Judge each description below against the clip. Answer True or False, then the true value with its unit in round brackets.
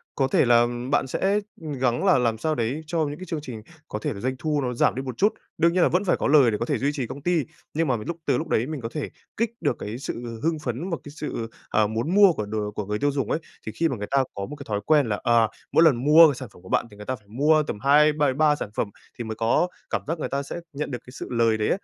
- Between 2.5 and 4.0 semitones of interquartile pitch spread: False (5.1 semitones)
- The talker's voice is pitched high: False (140 Hz)